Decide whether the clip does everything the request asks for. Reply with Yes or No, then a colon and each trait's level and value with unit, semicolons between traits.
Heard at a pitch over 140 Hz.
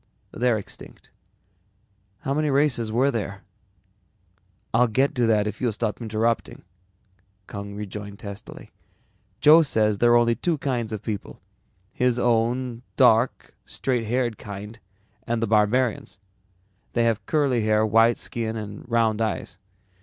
No: low, 115 Hz